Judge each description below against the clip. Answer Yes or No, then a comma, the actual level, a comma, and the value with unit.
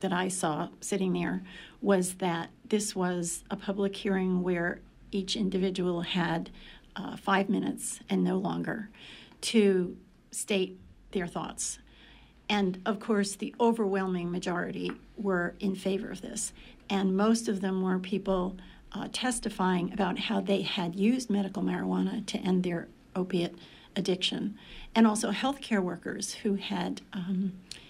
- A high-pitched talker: Yes, high, 195 Hz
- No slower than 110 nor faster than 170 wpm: Yes, average, 140 wpm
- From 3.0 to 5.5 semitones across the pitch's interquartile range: No, narrow, 2.5 semitones